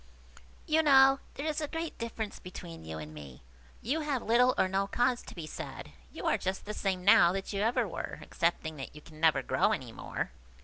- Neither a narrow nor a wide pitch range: No, wide, 8.6 semitones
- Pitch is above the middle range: Yes, high, 200 Hz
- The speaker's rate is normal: No, fast, 215 wpm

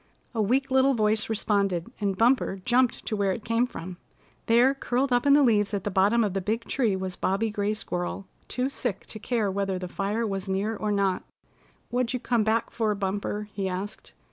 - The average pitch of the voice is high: Yes, high, 210 Hz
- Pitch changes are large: No, average, 3.3 semitones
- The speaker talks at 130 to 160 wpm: No, fast, 205 wpm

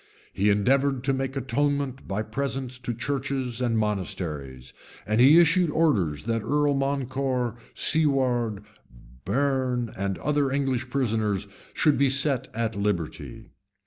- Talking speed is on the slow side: Yes, slow, 125 wpm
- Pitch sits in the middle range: No, low, 130 Hz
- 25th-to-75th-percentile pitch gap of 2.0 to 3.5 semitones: No, average, 4.3 semitones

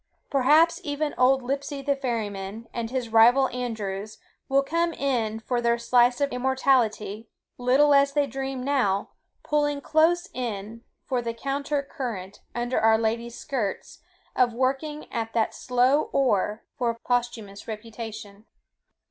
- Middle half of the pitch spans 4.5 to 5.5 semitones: No, average, 3.6 semitones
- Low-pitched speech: No, high, 245 Hz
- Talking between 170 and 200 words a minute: No, slow, 135 wpm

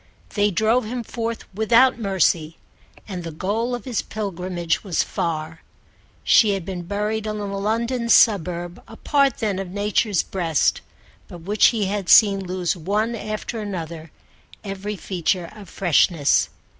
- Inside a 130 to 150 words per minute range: Yes, average, 145 wpm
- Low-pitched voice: No, high, 200 Hz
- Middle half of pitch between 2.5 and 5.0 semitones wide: Yes, average, 3.7 semitones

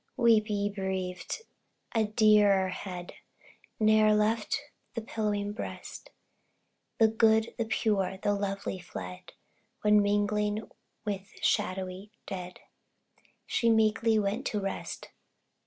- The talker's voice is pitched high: Yes, high, 210 Hz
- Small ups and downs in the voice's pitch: Yes, narrow, 2.0 semitones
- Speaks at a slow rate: Yes, slow, 110 wpm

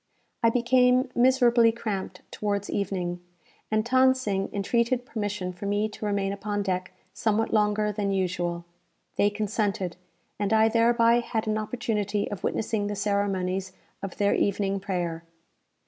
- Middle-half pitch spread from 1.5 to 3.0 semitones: Yes, narrow, 2.6 semitones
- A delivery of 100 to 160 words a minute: Yes, average, 140 wpm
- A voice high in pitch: Yes, high, 205 Hz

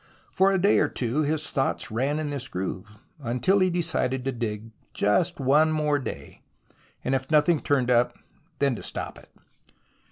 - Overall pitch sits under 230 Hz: Yes, medium, 140 Hz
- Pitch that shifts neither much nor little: Yes, average, 4.1 semitones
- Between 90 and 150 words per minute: No, average, 170 wpm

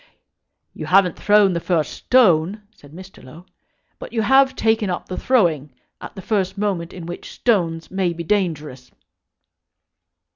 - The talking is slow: No, average, 150 wpm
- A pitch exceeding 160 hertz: Yes, medium, 185 Hz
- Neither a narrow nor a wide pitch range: Yes, average, 4.0 semitones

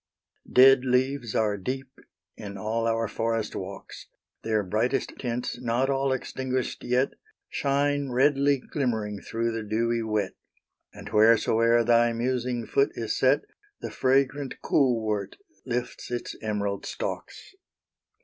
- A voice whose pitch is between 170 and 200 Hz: No, low, 120 Hz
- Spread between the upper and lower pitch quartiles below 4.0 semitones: Yes, average, 3.1 semitones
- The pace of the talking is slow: Yes, slow, 125 wpm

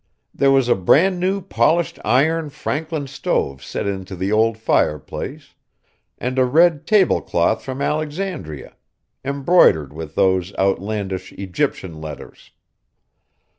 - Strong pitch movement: Yes, wide, 8.8 semitones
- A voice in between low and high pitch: No, low, 125 Hz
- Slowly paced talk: Yes, slow, 120 wpm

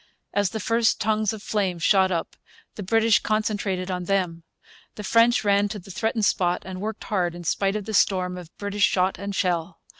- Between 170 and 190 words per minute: No, average, 200 wpm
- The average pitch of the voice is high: Yes, high, 200 Hz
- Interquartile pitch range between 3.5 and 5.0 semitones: No, average, 2.8 semitones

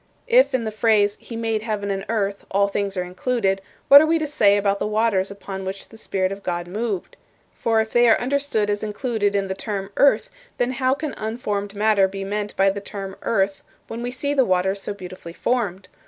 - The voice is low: No, high, 205 Hz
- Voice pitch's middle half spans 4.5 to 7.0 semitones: No, average, 3.0 semitones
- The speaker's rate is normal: No, fast, 215 wpm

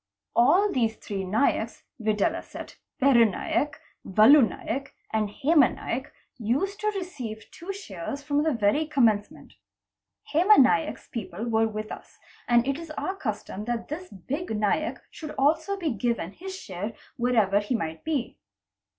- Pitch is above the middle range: Yes, high, 240 Hz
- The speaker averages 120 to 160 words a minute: Yes, average, 150 wpm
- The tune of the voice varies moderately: No, wide, 6.2 semitones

